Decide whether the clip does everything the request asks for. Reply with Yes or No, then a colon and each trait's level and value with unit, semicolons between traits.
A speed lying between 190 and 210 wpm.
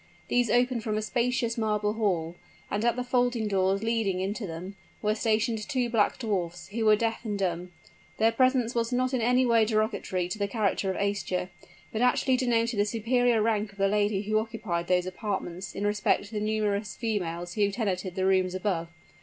Yes: average, 195 wpm